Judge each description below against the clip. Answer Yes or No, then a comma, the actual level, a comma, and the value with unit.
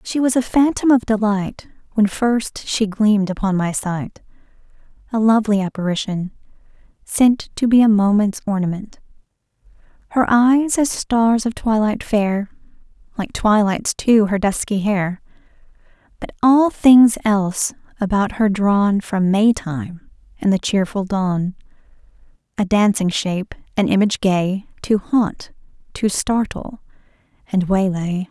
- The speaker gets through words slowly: Yes, slow, 130 wpm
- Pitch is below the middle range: No, high, 210 Hz